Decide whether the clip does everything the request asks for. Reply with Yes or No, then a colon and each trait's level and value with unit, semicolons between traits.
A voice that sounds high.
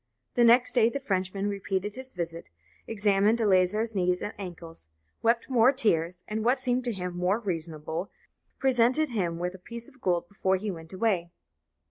Yes: high, 200 Hz